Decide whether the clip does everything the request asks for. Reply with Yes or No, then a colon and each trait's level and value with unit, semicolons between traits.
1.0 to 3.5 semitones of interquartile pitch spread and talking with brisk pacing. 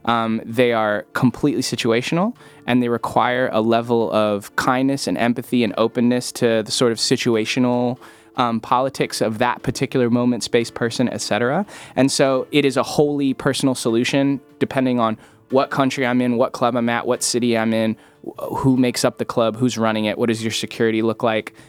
No: narrow, 2.4 semitones; average, 185 wpm